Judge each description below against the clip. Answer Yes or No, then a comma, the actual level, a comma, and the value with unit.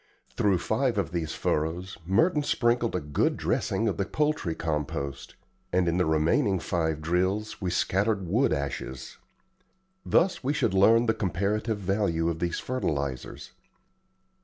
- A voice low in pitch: Yes, very low, 95 Hz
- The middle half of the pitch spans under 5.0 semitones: No, average, 5.3 semitones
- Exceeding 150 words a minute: No, average, 140 wpm